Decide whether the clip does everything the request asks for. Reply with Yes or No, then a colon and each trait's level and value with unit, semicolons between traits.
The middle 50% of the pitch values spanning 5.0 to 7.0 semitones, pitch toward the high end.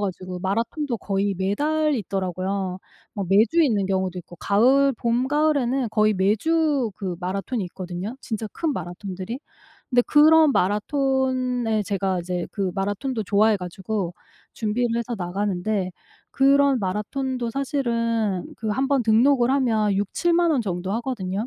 Yes: wide, 5.4 semitones; high, 220 Hz